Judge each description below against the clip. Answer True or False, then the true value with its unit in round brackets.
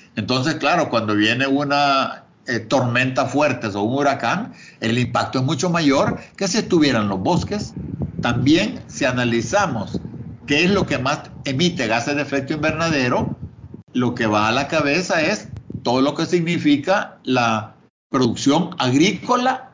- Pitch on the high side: False (140 Hz)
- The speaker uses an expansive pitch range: False (4.6 semitones)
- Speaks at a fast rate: False (145 wpm)